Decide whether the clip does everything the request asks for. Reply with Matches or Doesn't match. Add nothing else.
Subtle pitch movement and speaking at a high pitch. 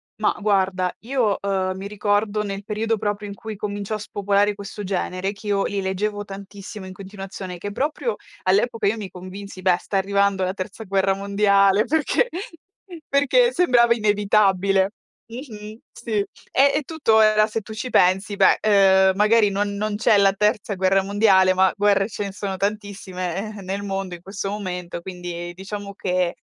Matches